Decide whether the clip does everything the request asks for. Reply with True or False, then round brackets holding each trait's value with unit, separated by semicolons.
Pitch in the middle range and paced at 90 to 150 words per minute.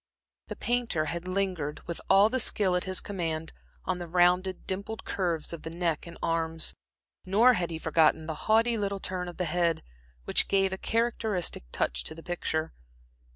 False (180 Hz; 180 wpm)